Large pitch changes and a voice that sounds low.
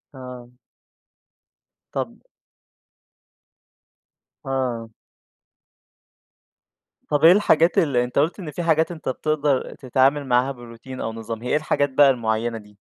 No: average, 3.7 semitones; low, 130 Hz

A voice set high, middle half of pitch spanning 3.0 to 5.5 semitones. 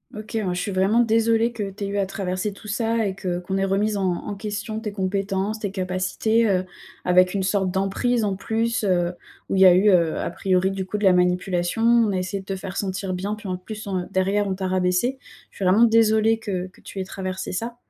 No: high, 195 Hz; narrow, 2.5 semitones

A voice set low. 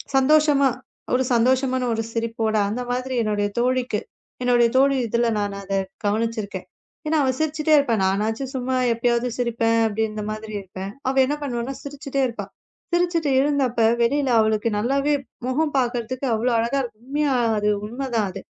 No: high, 245 Hz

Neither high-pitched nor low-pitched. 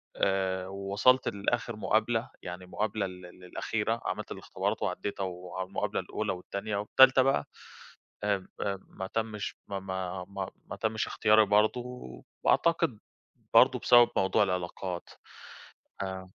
No: low, 100 Hz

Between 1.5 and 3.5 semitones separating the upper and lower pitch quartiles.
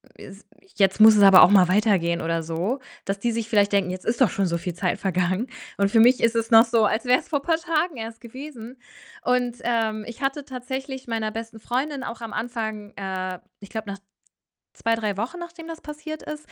No: average, 4.4 semitones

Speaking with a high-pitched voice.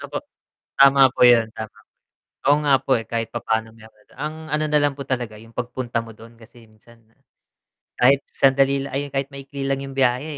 No: low, 130 Hz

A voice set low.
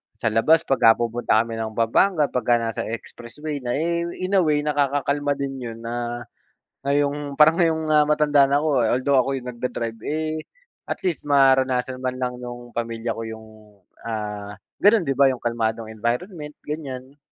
Yes: low, 130 Hz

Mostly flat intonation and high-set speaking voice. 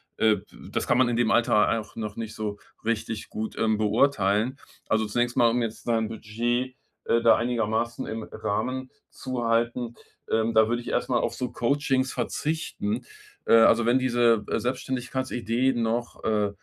No: narrow, 2.0 semitones; low, 115 Hz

